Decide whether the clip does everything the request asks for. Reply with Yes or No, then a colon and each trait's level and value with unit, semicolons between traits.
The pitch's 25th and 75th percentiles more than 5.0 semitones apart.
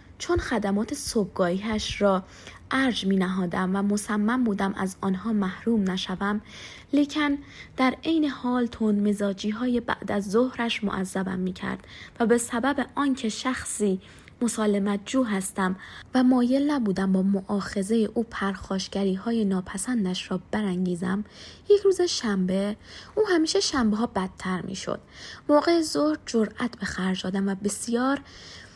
No: average, 4.5 semitones